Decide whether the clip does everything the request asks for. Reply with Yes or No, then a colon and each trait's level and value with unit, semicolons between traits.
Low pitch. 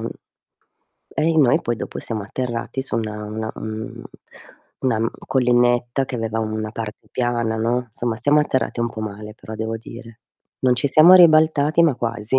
Yes: low, 120 Hz